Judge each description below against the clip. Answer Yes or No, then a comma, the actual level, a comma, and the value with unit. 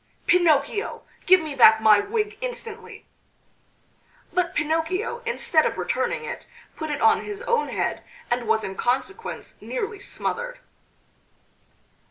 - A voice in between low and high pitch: No, very high, 365 Hz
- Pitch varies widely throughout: Yes, wide, 7.6 semitones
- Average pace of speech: No, slow, 125 wpm